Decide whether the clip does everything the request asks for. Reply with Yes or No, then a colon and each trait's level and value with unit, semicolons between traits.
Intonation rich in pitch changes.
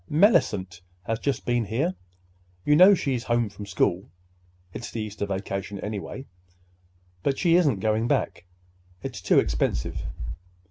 Yes: wide, 5.8 semitones